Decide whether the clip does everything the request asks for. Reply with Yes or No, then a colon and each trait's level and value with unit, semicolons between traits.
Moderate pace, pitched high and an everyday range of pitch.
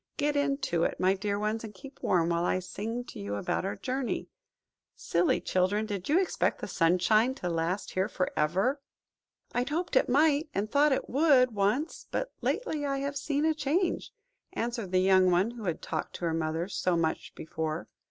No: average, 190 wpm; high, 210 Hz; wide, 7.4 semitones